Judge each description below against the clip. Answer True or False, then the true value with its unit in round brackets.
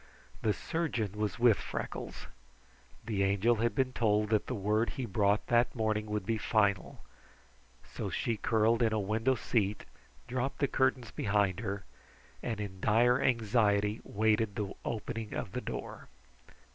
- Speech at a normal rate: True (150 wpm)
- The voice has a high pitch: False (110 Hz)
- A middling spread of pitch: False (2.3 semitones)